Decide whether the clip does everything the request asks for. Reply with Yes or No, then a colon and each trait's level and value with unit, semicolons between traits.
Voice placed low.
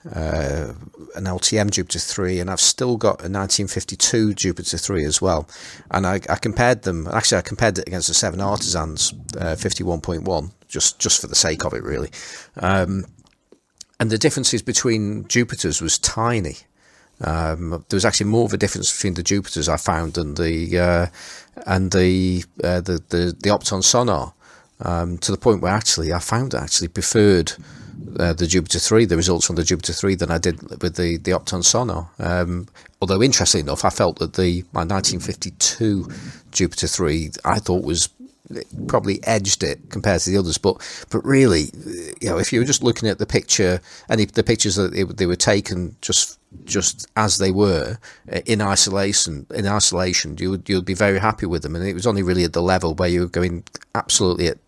Yes: very low, 95 Hz